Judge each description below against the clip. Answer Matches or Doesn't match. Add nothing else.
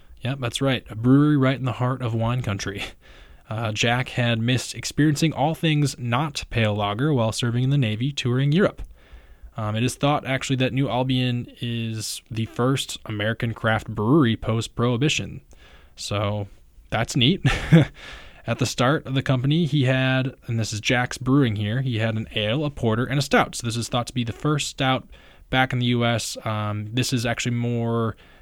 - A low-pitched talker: Matches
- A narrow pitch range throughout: Doesn't match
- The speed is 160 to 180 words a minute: Doesn't match